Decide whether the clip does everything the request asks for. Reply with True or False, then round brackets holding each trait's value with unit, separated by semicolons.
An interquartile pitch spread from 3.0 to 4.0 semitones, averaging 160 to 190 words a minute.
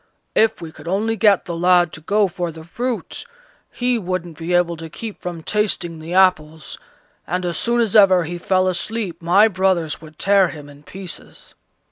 True (3.3 semitones; 185 wpm)